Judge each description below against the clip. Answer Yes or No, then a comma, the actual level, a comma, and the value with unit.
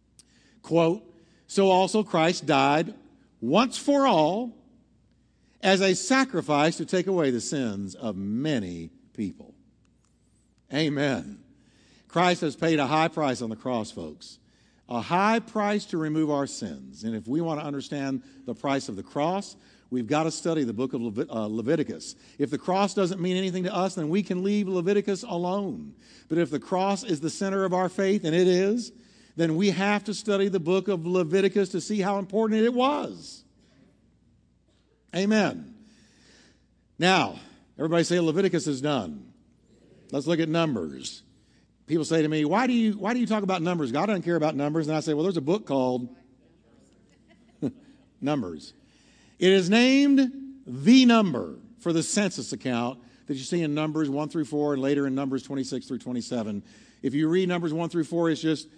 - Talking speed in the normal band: Yes, average, 175 wpm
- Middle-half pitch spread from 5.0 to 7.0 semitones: Yes, wide, 5.6 semitones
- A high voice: No, medium, 170 Hz